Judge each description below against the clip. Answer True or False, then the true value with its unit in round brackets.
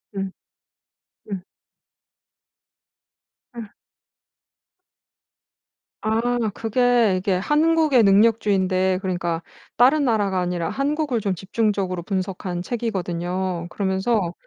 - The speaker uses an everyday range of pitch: True (4.0 semitones)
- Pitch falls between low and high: False (195 Hz)